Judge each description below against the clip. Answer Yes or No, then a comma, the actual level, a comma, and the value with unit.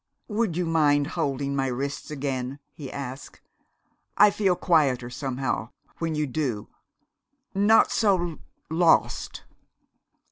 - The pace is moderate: No, slow, 110 wpm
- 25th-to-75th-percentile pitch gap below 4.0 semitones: No, average, 4.4 semitones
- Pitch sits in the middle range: Yes, medium, 145 Hz